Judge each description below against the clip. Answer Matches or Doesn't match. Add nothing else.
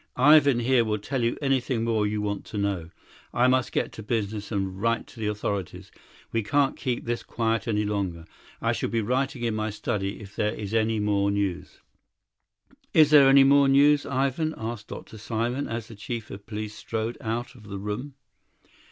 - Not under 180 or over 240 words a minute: Matches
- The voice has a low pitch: Matches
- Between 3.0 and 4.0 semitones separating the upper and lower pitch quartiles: Matches